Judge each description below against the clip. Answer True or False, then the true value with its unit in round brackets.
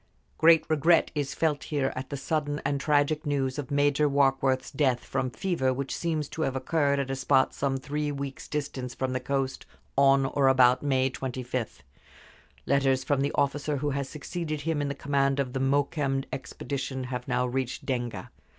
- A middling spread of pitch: False (1.7 semitones)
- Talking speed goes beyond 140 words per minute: True (180 wpm)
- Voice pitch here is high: False (140 Hz)